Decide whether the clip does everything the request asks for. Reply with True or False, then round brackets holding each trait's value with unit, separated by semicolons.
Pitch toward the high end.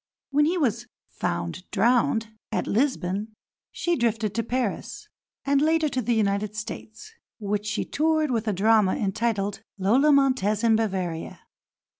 True (225 Hz)